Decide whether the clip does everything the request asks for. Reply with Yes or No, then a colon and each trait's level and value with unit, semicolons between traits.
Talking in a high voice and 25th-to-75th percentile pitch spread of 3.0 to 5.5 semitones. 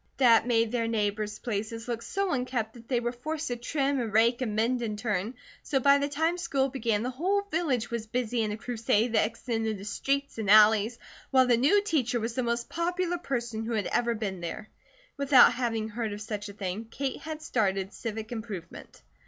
Yes: high, 235 Hz; average, 3.3 semitones